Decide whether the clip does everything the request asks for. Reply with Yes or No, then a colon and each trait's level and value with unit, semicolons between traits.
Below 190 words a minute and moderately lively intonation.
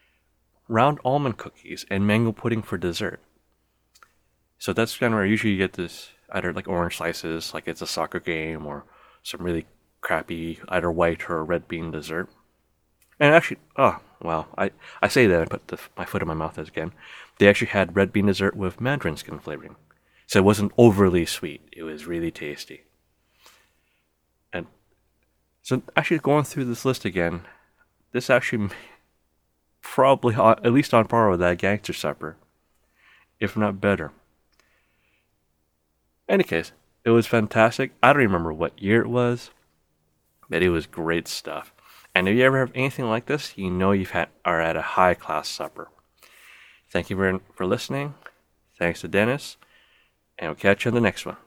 No: average, 175 wpm; wide, 6.1 semitones